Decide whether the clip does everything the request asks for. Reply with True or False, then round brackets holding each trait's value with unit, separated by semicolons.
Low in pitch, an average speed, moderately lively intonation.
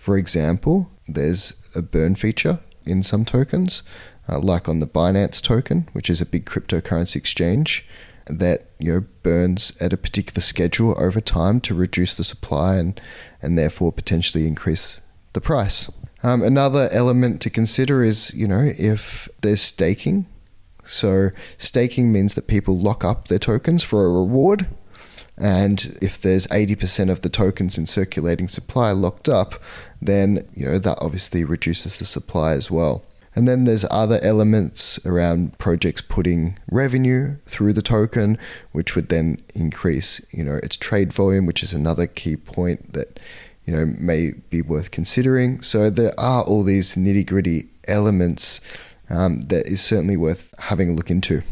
True (95 Hz; 160 wpm; 4.3 semitones)